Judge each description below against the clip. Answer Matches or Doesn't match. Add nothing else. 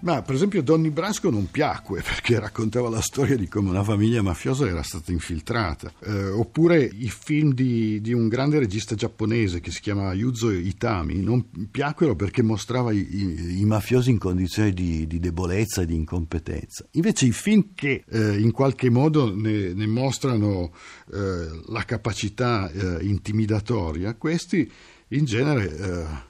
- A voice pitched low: Matches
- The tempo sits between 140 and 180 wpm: Matches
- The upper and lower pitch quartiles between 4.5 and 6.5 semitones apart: Matches